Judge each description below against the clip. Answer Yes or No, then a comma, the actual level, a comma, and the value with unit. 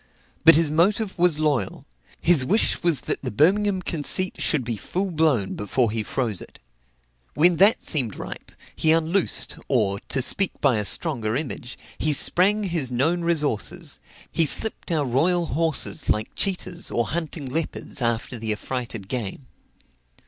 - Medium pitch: Yes, medium, 150 Hz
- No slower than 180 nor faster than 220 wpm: No, average, 155 wpm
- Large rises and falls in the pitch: Yes, wide, 6.1 semitones